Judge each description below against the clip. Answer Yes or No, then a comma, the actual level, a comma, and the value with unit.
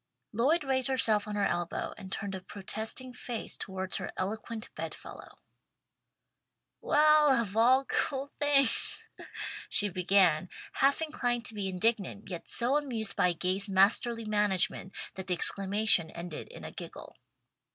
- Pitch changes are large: No, average, 4.9 semitones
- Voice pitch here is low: No, high, 210 Hz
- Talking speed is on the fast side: No, average, 140 wpm